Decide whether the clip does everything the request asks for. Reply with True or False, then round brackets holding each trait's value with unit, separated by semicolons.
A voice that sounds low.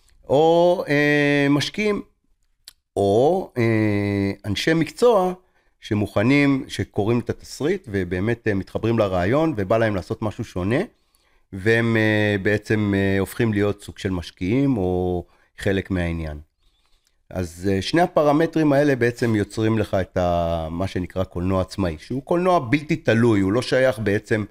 True (105 Hz)